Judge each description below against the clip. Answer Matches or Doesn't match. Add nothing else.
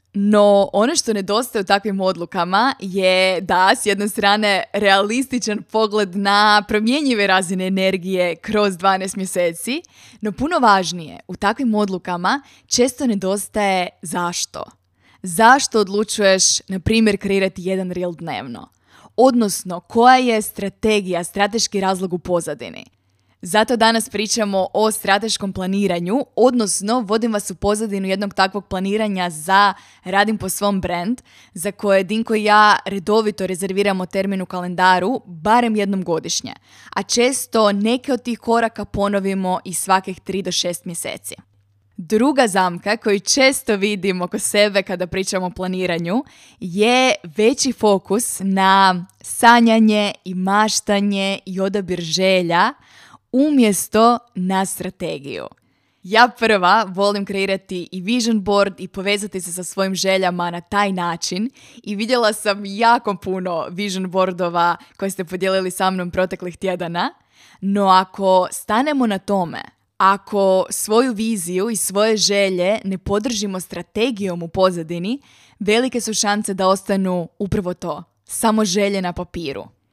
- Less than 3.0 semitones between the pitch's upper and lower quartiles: Matches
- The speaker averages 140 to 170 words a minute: Doesn't match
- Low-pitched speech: Doesn't match